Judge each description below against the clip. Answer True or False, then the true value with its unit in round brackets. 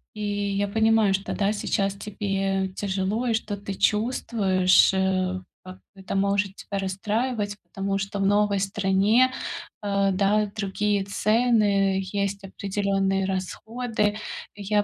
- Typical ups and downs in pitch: False (1.4 semitones)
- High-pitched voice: True (200 Hz)